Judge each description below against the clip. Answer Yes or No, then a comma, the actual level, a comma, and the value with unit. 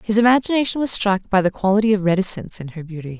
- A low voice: No, high, 200 Hz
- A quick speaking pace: Yes, fast, 225 wpm